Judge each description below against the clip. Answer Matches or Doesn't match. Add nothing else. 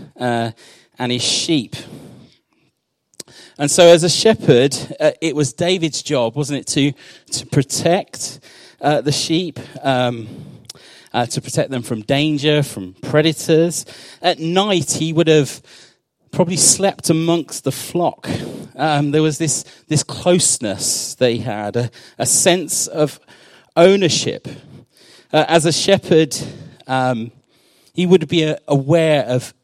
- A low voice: Doesn't match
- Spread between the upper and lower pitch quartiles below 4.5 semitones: Matches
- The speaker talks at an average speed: Doesn't match